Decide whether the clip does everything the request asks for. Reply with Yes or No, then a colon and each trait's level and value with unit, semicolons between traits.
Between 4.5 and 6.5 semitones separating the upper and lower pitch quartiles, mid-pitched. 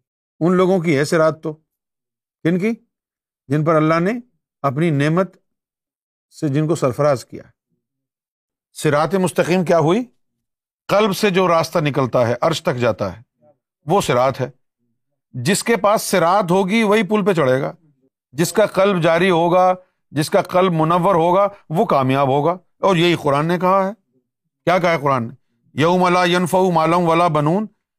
Yes: average, 5.1 semitones; medium, 165 Hz